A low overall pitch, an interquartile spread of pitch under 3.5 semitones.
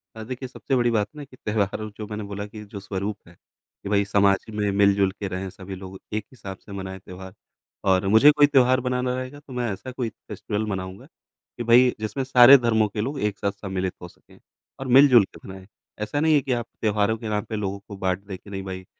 No: low, 105 Hz; average, 4.1 semitones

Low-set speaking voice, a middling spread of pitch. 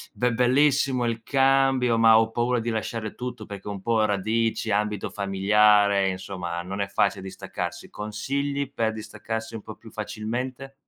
Yes: low, 110 Hz; average, 3.2 semitones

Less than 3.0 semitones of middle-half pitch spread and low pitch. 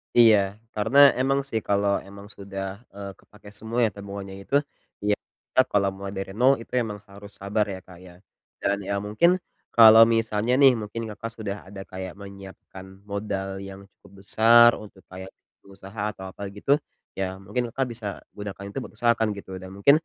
Yes: narrow, 2.5 semitones; low, 100 Hz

